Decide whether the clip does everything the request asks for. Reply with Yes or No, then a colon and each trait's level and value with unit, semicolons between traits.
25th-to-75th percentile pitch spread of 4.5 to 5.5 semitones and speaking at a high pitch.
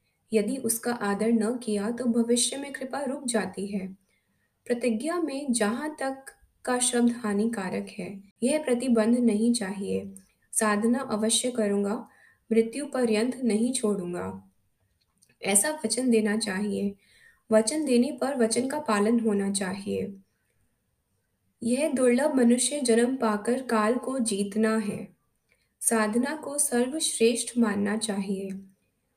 No: average, 3.6 semitones; high, 225 Hz